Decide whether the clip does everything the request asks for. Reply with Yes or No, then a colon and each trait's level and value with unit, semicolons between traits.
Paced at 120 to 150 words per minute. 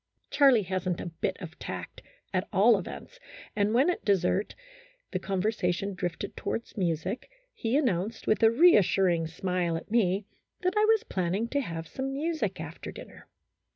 No: average, 165 wpm